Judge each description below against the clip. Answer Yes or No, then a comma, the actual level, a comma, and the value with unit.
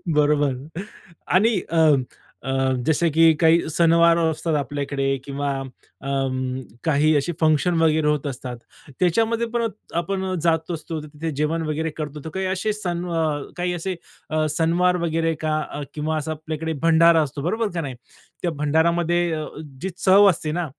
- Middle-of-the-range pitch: Yes, medium, 160 Hz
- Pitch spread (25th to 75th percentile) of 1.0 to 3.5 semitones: Yes, narrow, 2.4 semitones